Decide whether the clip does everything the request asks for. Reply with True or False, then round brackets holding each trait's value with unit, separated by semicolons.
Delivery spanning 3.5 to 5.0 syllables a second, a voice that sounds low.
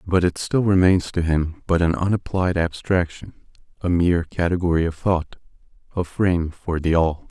True (4.9 syllables/s; 85 Hz)